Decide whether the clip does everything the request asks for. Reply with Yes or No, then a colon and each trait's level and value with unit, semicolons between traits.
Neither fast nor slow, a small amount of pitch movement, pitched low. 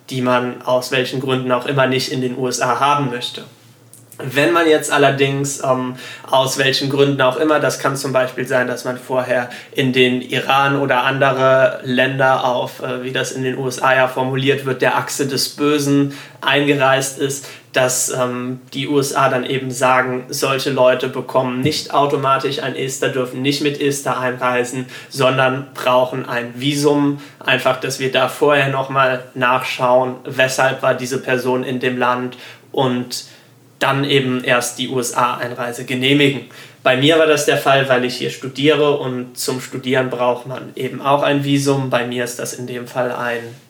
Yes: average, 170 wpm; narrow, 1.5 semitones; low, 130 Hz